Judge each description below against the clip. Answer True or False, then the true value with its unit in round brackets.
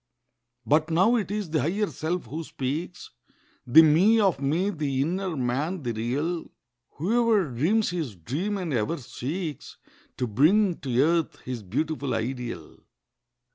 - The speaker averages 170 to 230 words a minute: False (135 wpm)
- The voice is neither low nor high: True (155 Hz)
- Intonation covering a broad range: True (5.9 semitones)